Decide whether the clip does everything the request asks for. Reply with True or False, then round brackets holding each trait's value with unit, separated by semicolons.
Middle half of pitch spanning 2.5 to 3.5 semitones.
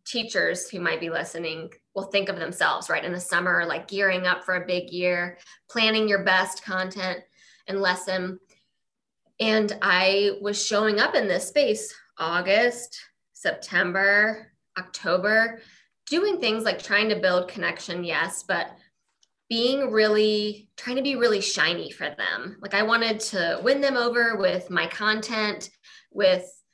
True (2.9 semitones)